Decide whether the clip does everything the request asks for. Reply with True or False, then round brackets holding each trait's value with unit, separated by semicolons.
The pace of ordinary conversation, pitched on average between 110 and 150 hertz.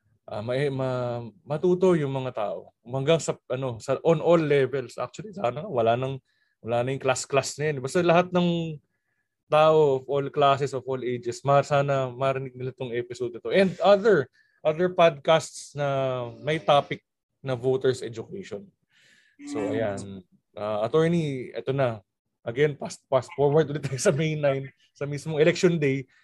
False (160 wpm; 140 Hz)